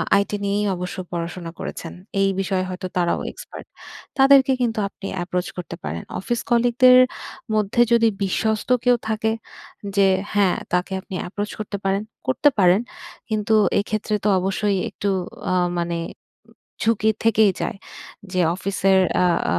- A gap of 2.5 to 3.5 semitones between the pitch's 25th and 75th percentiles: Yes, average, 3.1 semitones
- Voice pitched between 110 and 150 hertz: No, high, 200 Hz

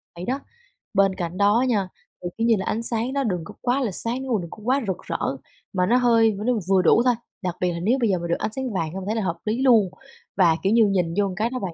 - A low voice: No, high, 210 Hz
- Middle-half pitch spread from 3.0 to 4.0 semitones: No, average, 4.6 semitones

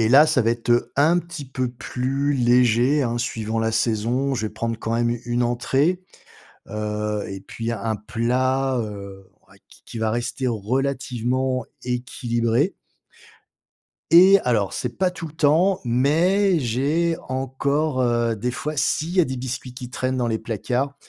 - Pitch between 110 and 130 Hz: Yes, low, 125 Hz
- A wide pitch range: No, average, 3.3 semitones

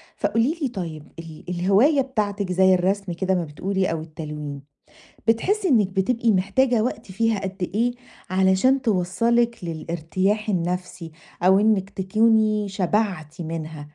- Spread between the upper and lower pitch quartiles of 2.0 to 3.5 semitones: No, average, 4.2 semitones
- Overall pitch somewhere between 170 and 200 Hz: Yes, high, 190 Hz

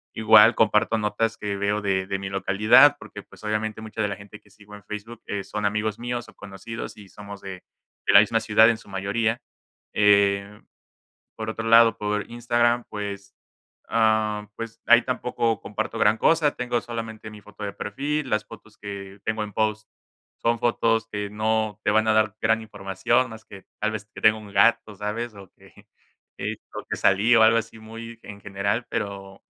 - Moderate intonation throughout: No, narrow, 1.8 semitones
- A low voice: Yes, low, 110 Hz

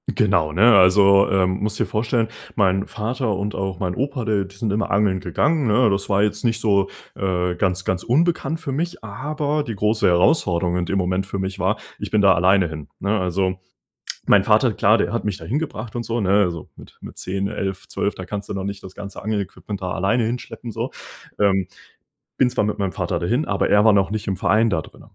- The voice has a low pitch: Yes, low, 100 Hz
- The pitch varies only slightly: No, average, 3.1 semitones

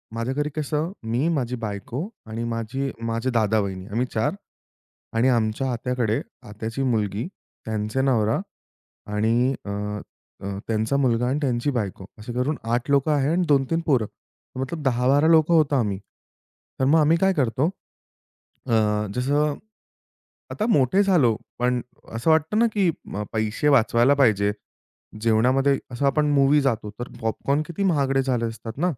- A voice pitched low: Yes, low, 130 Hz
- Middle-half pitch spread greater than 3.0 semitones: Yes, average, 4.2 semitones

